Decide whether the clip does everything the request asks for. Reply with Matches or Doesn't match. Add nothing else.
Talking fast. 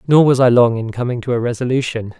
Matches